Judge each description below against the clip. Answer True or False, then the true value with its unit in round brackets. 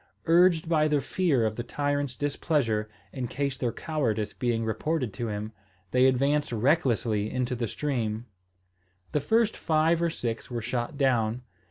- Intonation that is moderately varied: True (4.7 semitones)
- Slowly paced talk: False (155 wpm)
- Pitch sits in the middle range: False (130 Hz)